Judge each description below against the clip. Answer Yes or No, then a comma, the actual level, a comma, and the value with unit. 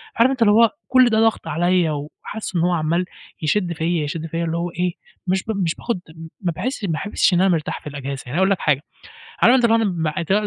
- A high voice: No, medium, 175 Hz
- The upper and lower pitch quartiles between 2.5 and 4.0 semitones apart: No, average, 4.4 semitones